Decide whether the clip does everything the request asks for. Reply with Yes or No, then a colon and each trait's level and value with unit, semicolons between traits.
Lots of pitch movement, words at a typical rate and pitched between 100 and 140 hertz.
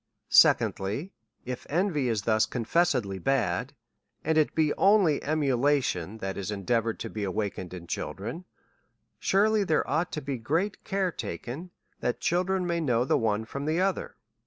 Yes: wide, 7.8 semitones; average, 155 wpm; low, 135 Hz